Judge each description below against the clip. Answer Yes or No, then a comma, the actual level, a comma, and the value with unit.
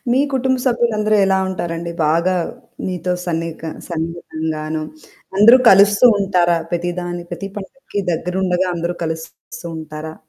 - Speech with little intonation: No, average, 3.1 semitones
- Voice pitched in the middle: Yes, medium, 175 Hz